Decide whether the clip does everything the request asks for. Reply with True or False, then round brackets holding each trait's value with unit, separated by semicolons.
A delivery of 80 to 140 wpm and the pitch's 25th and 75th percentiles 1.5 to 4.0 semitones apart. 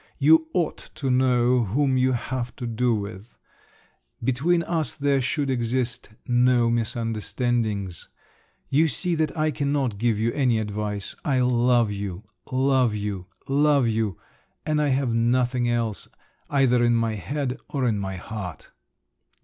True (135 wpm; 3.5 semitones)